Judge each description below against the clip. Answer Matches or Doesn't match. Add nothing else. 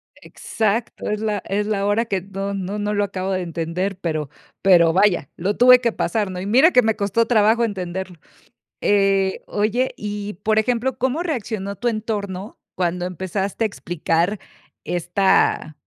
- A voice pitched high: Matches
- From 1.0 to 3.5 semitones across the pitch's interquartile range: Matches